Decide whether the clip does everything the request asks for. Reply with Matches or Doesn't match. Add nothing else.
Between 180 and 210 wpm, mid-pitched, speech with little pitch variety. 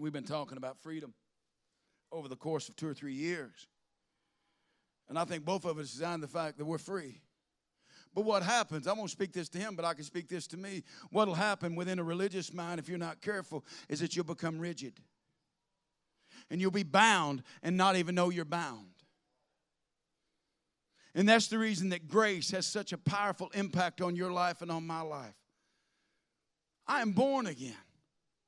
Doesn't match